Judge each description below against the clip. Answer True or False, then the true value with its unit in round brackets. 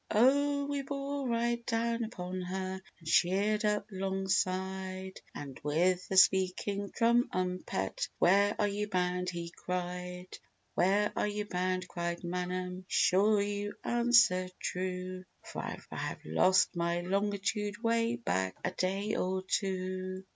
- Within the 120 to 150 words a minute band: True (140 wpm)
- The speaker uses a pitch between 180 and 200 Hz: True (190 Hz)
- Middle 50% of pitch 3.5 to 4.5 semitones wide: False (2.4 semitones)